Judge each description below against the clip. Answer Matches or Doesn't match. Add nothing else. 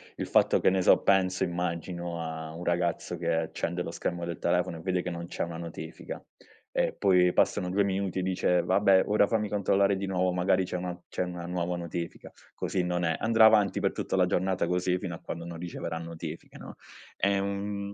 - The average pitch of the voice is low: Matches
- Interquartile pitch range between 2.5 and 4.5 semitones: Doesn't match